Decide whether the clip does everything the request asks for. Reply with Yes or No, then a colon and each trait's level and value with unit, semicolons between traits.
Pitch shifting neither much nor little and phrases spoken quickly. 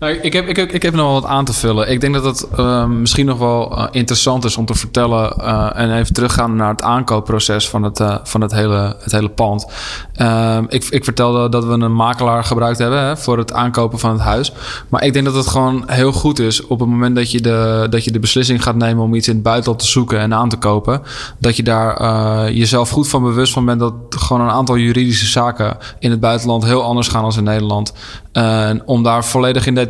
No: narrow, 2.1 semitones; fast, 245 wpm